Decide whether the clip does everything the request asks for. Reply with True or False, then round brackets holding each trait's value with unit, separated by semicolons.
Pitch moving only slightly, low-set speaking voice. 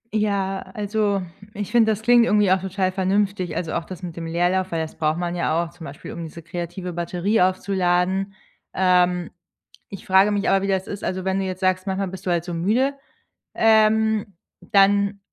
False (2.3 semitones; 190 Hz)